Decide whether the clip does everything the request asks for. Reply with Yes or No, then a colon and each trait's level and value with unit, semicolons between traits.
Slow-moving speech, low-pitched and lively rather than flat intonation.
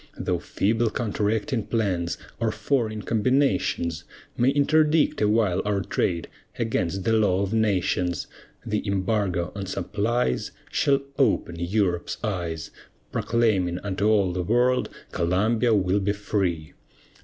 No: slow, 120 wpm; low, 105 Hz; average, 3.9 semitones